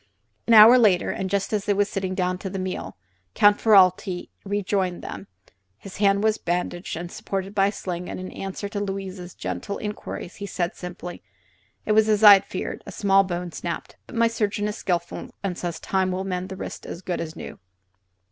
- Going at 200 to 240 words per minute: Yes, fast, 205 wpm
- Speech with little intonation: Yes, narrow, 2.3 semitones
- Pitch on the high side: Yes, high, 195 Hz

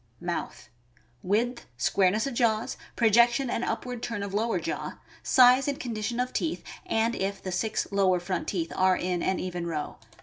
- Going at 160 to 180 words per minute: Yes, average, 175 wpm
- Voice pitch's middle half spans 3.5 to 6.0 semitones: Yes, average, 4.3 semitones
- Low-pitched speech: No, high, 215 Hz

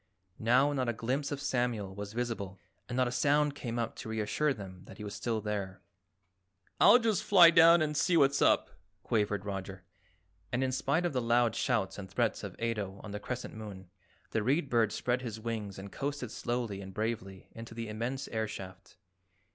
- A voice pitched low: Yes, low, 115 Hz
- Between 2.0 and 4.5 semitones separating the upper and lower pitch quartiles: Yes, average, 4.2 semitones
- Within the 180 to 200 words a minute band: Yes, average, 195 wpm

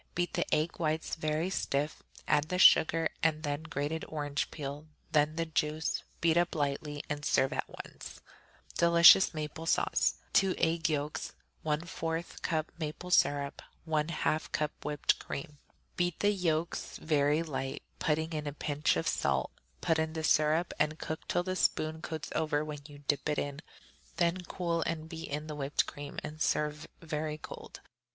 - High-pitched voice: No, medium, 155 Hz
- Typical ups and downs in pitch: No, narrow, 1.8 semitones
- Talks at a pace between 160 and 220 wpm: Yes, average, 165 wpm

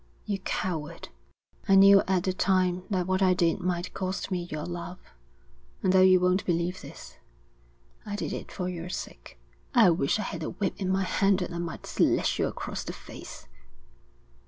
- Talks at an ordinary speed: Yes, average, 185 wpm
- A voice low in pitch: No, medium, 185 Hz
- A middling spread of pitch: No, narrow, 1.5 semitones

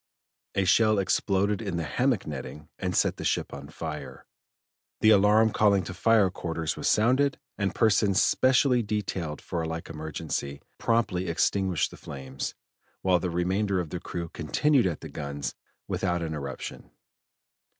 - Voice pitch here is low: Yes, very low, 95 Hz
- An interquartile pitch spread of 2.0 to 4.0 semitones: No, average, 4.8 semitones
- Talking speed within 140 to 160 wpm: Yes, average, 150 wpm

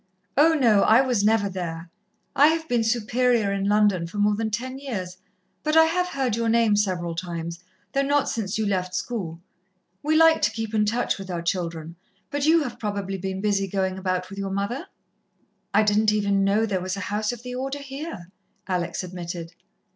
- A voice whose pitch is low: No, high, 210 Hz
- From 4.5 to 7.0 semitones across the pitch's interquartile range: Yes, average, 4.9 semitones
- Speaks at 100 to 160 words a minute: No, average, 195 wpm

